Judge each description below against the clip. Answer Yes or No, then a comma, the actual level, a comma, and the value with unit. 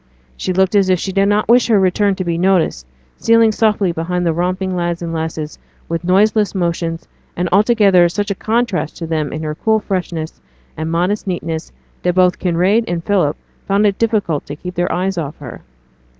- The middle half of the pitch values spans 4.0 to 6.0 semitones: No, average, 3.3 semitones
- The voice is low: No, medium, 180 Hz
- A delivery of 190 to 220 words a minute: Yes, average, 195 wpm